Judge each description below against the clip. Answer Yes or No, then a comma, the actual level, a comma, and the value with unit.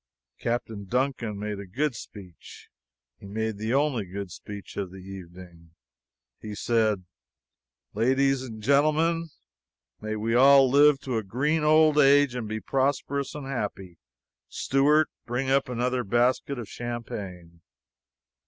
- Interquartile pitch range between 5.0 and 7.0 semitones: Yes, average, 5.3 semitones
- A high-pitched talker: No, low, 120 Hz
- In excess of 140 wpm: No, slow, 135 wpm